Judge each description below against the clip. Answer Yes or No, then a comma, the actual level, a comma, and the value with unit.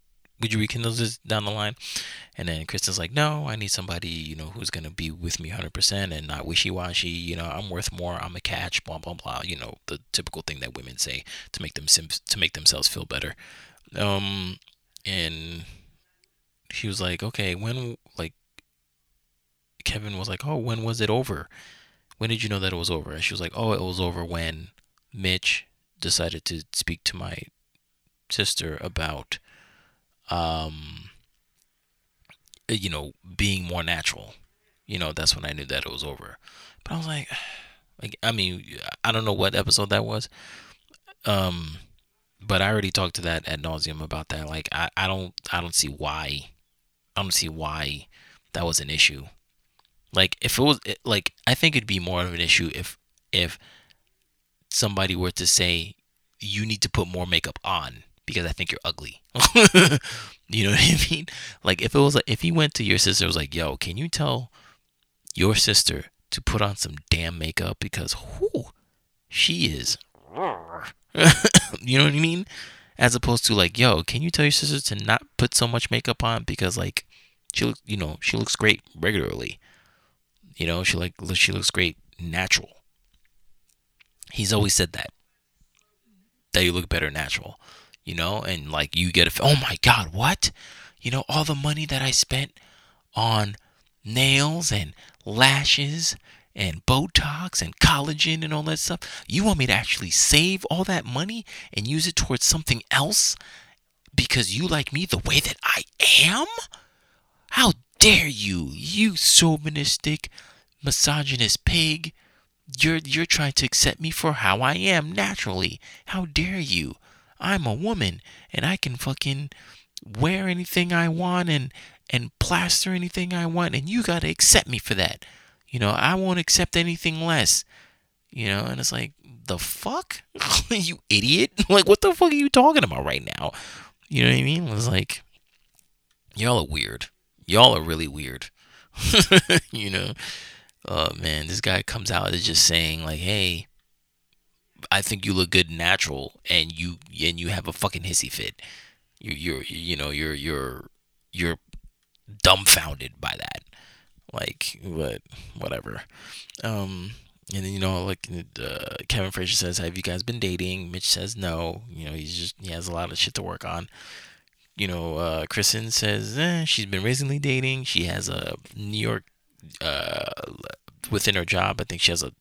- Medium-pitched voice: No, very low, 95 Hz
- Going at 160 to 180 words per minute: Yes, average, 175 wpm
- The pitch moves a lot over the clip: Yes, wide, 7.9 semitones